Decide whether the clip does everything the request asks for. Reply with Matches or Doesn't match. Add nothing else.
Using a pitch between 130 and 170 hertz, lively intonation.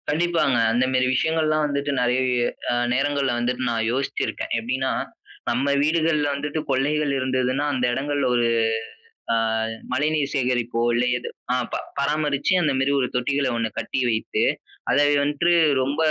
Doesn't match